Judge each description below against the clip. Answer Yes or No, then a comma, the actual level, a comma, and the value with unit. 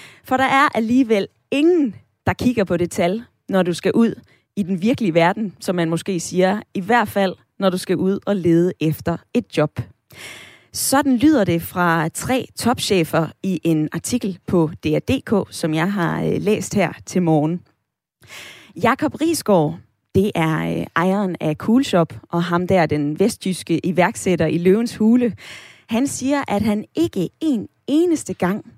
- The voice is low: No, high, 190 Hz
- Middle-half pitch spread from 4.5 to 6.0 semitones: Yes, wide, 5.5 semitones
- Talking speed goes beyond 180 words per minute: No, average, 160 wpm